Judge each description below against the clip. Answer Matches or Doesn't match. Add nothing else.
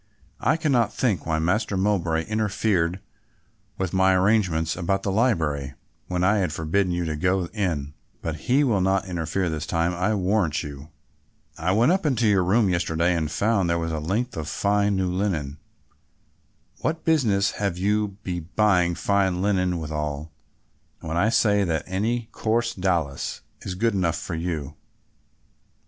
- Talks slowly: Doesn't match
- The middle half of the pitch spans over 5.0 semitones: Doesn't match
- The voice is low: Matches